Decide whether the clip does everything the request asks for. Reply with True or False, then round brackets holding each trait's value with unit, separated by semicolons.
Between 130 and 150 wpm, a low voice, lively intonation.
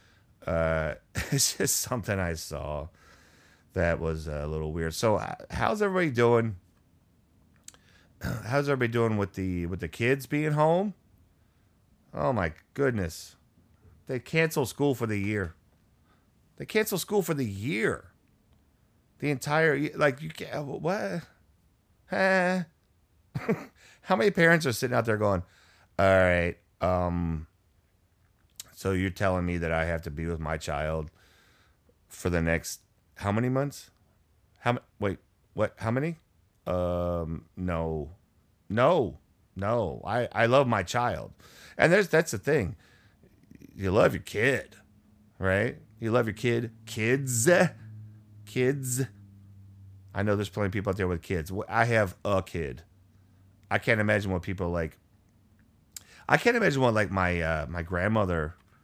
True (140 wpm; 100 Hz; 5.9 semitones)